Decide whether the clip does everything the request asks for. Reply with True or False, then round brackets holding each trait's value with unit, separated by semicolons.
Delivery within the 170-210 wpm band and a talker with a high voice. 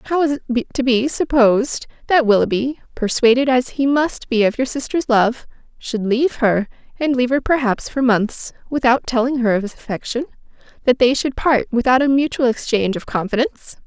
True (175 wpm; 250 Hz)